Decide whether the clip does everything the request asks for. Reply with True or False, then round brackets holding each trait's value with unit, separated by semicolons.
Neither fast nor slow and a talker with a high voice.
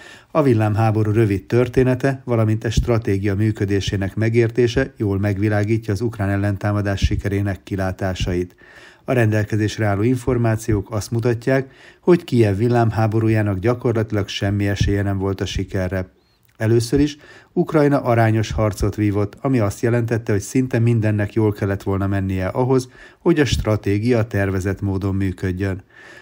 False (125 wpm; 110 Hz)